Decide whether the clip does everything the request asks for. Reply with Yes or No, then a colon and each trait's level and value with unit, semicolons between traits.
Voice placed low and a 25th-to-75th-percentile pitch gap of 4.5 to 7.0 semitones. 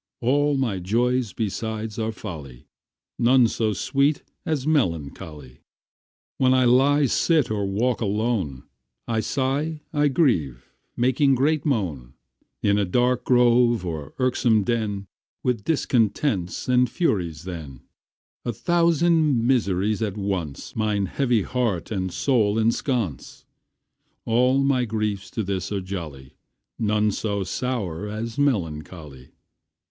Yes: low, 110 Hz; average, 5.1 semitones